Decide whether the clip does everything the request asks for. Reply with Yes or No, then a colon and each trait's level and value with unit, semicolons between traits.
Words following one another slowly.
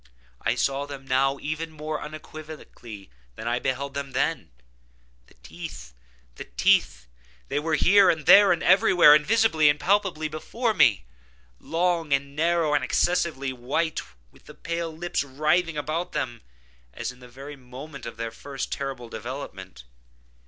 No: average, 145 wpm